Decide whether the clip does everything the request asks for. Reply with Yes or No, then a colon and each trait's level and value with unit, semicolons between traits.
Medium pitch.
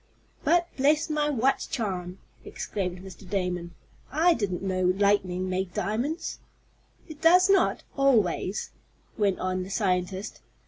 No: high, 200 Hz